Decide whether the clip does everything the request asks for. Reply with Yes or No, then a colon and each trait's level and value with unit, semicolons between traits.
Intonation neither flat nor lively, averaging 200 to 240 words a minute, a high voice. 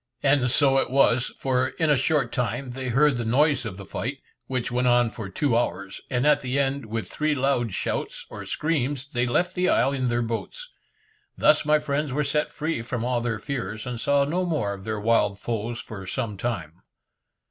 No: average, 3.7 semitones; fast, 205 wpm; low, 125 Hz